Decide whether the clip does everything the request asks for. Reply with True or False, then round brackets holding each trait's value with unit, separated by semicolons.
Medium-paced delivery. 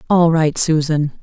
True (145 wpm)